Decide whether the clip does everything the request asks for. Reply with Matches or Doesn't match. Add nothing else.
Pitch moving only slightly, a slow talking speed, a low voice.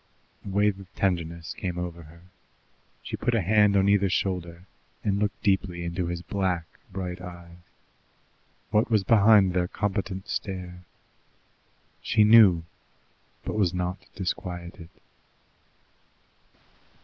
Matches